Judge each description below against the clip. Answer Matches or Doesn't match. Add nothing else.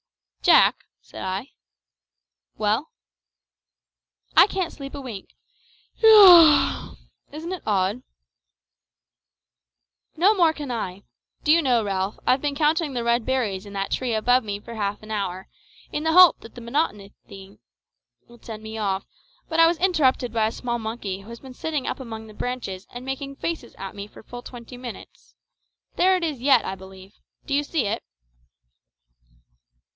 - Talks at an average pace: Matches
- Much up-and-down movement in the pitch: Matches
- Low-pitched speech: Doesn't match